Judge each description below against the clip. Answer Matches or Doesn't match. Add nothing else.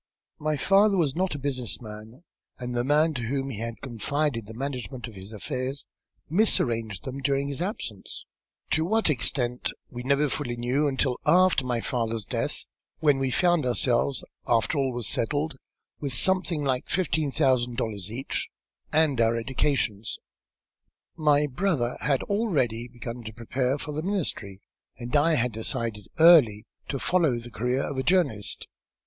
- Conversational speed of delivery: Matches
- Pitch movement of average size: Matches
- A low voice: Matches